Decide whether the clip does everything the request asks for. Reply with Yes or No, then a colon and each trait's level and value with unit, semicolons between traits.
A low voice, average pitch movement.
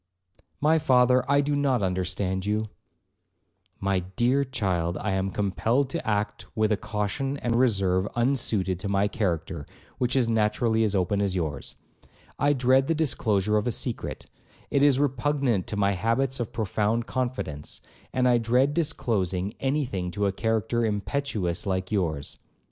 Yes: low, 110 Hz; average, 5.0 semitones